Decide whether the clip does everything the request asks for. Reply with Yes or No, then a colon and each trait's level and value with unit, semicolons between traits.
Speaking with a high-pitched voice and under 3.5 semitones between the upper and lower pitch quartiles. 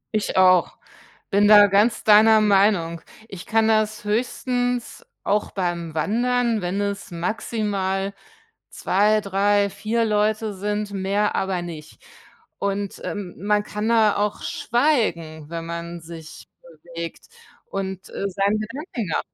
Yes: high, 205 Hz; average, 2.8 semitones